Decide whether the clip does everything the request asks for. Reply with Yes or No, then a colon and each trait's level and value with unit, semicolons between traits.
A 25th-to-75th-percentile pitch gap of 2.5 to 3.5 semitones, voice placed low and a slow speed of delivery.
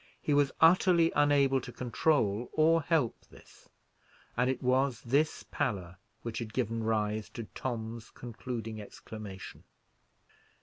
No: average, 4.5 semitones; low, 125 Hz; slow, 125 wpm